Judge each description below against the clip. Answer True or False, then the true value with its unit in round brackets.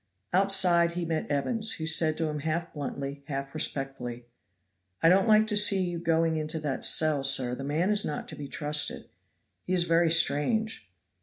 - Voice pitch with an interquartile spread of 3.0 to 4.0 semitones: True (3.7 semitones)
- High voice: False (160 Hz)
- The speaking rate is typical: True (180 wpm)